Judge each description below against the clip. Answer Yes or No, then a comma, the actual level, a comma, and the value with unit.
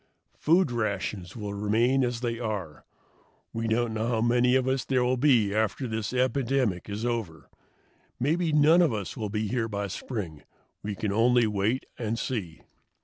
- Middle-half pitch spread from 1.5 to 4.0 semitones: Yes, average, 3.3 semitones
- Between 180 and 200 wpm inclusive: No, average, 170 wpm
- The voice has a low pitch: Yes, low, 115 Hz